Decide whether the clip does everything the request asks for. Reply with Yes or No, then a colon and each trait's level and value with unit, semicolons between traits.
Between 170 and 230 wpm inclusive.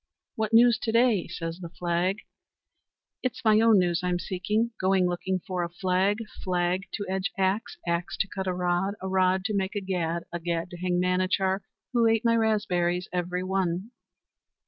Yes: average, 180 wpm